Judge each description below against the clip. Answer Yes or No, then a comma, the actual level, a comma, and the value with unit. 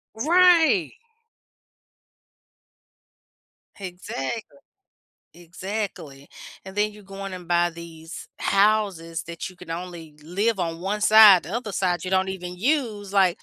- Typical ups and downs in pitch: Yes, average, 3.5 semitones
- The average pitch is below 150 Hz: No, high, 190 Hz